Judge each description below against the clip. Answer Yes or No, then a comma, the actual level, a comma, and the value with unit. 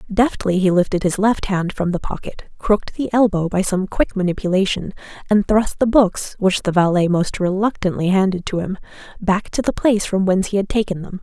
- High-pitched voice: Yes, high, 195 Hz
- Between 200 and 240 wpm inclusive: Yes, fast, 205 wpm